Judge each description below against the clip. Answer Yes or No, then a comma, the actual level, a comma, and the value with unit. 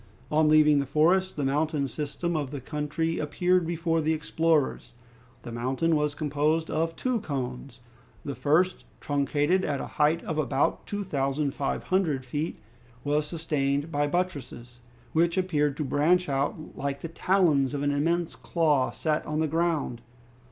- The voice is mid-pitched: Yes, medium, 150 Hz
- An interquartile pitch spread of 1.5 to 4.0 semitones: Yes, average, 2.7 semitones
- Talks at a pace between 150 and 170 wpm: Yes, average, 160 wpm